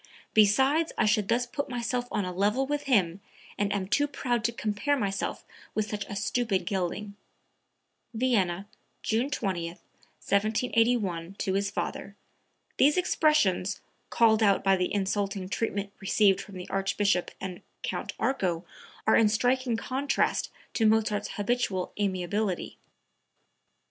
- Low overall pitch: No, high, 210 Hz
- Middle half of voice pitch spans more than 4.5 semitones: No, average, 3.8 semitones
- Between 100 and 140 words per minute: Yes, slow, 135 wpm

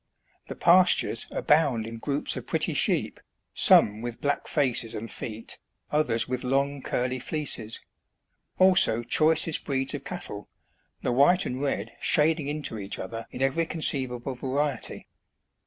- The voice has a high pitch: No, low, 135 Hz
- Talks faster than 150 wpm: No, average, 140 wpm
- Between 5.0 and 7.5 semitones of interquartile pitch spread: No, average, 4.4 semitones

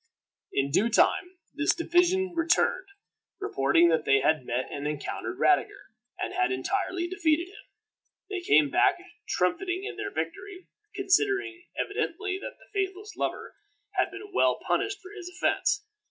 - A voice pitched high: Yes, very high, 360 Hz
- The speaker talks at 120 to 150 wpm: Yes, average, 145 wpm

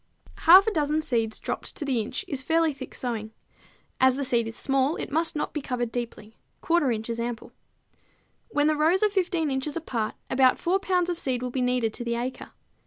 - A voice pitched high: Yes, very high, 265 Hz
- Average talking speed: No, fast, 210 wpm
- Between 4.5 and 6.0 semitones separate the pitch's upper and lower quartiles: Yes, average, 5.1 semitones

